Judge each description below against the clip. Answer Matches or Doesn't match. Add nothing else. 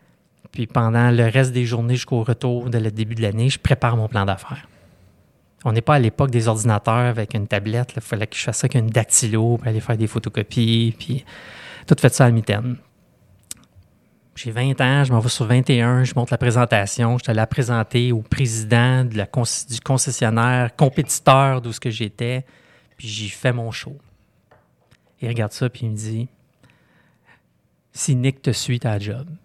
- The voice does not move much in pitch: Matches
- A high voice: Doesn't match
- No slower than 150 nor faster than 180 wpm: Doesn't match